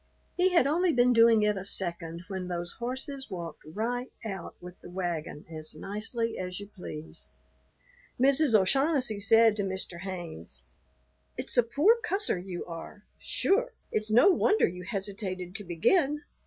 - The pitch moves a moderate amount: No, wide, 6.0 semitones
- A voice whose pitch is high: Yes, high, 205 Hz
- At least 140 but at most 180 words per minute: Yes, average, 155 wpm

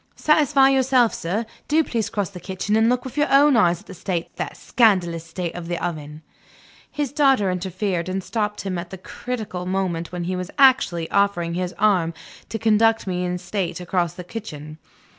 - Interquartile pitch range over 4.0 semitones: Yes, average, 4.5 semitones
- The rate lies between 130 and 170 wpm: No, average, 190 wpm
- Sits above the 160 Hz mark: Yes, high, 190 Hz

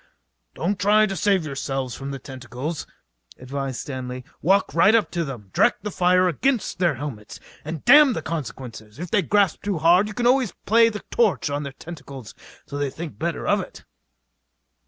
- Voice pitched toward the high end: No, medium, 165 Hz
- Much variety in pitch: Yes, wide, 6.8 semitones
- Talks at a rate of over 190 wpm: No, average, 180 wpm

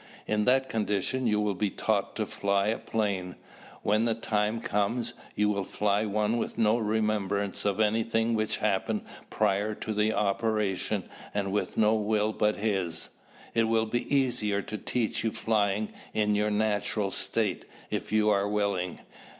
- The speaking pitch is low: Yes, low, 105 Hz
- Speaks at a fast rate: No, average, 160 wpm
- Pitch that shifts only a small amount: Yes, narrow, 1.5 semitones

